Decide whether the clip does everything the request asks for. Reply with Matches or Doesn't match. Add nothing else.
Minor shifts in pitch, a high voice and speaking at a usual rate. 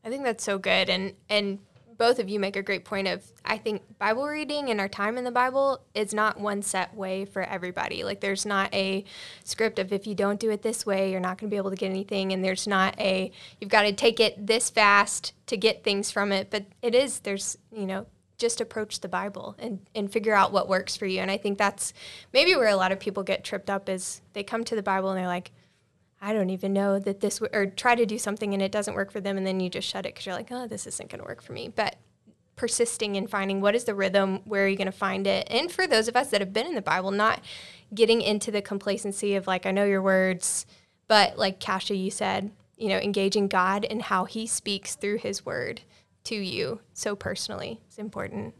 Doesn't match